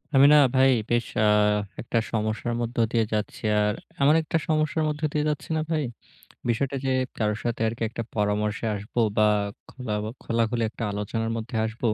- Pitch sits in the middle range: No, low, 115 Hz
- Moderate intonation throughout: Yes, average, 3.7 semitones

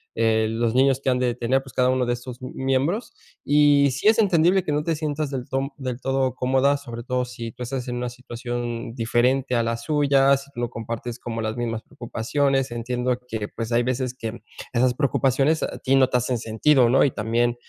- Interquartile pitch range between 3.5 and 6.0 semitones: No, narrow, 2.4 semitones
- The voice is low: Yes, low, 125 Hz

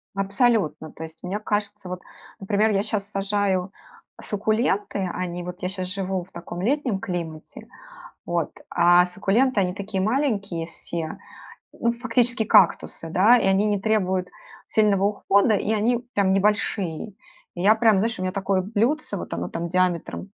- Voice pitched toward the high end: Yes, high, 195 Hz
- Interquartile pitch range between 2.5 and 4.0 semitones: Yes, average, 2.9 semitones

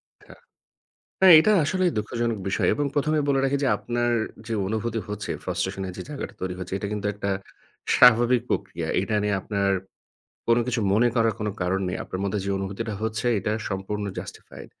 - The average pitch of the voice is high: No, low, 110 Hz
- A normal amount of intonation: Yes, average, 3.4 semitones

